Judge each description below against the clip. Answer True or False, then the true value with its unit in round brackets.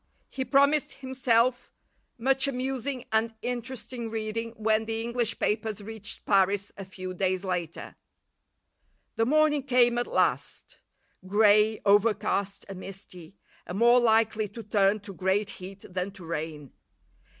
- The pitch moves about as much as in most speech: True (3.6 semitones)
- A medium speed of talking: False (130 wpm)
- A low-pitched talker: False (220 Hz)